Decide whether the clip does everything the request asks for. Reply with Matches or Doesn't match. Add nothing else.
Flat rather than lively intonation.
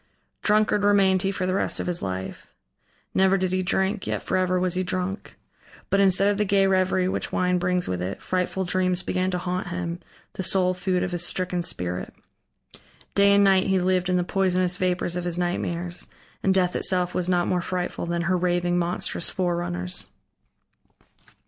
Matches